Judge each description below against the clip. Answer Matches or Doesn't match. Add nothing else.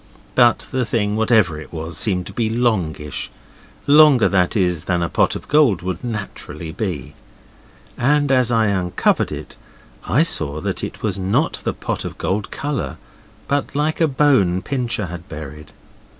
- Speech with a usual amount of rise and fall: Doesn't match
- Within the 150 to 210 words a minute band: Matches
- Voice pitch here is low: Matches